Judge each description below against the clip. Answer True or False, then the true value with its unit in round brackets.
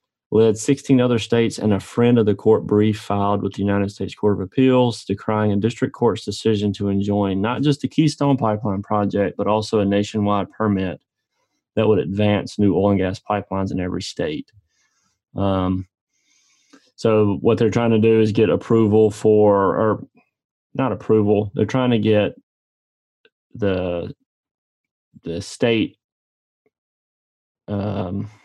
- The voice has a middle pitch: False (105 Hz)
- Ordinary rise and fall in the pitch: False (2.1 semitones)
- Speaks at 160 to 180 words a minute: False (150 wpm)